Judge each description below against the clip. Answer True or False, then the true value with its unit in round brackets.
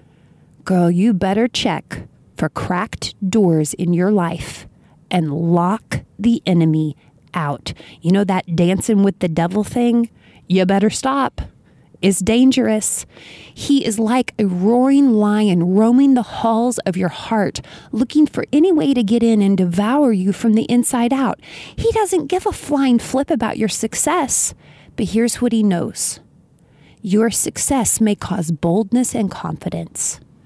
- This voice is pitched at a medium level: False (215 Hz)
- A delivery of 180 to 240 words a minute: False (150 wpm)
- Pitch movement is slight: False (4.9 semitones)